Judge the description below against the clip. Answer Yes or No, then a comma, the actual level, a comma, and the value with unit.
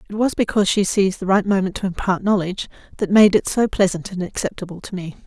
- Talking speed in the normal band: No, fast, 230 wpm